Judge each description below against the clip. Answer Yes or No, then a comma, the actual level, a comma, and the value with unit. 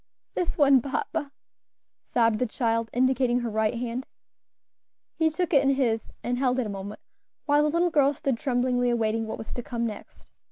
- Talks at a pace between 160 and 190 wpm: Yes, average, 185 wpm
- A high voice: Yes, high, 245 Hz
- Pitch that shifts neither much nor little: Yes, average, 3.3 semitones